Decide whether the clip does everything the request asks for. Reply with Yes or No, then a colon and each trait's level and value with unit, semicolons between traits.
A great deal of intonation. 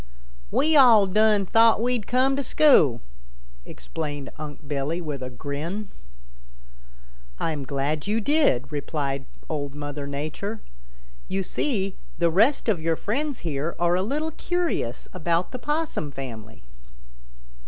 Yes: wide, 8.0 semitones